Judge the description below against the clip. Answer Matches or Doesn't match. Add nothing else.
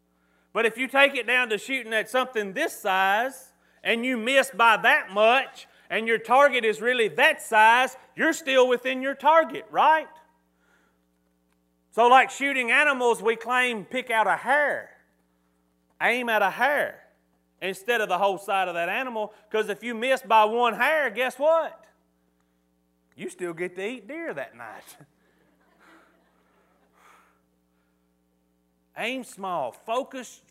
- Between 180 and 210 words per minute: Doesn't match